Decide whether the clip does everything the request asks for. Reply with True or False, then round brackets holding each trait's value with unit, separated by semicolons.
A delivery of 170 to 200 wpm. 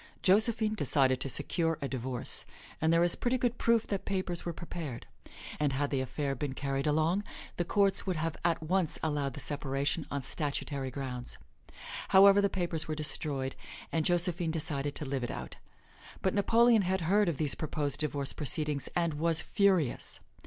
True (175 wpm)